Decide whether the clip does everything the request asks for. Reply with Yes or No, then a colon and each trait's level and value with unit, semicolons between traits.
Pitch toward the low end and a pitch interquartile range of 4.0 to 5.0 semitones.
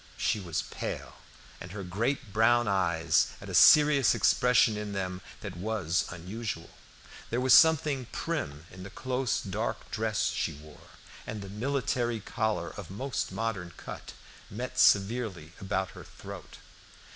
Yes: low, 105 Hz; average, 4.7 semitones